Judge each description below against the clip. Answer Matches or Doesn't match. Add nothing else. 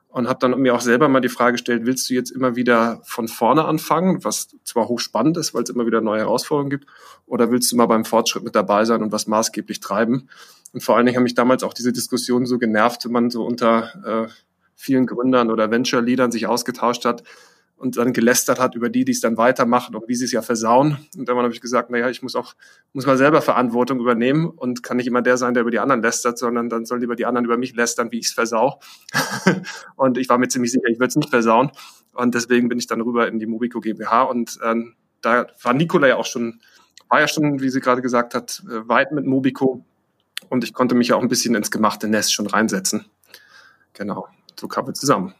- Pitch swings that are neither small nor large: Doesn't match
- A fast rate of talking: Matches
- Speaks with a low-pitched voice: Matches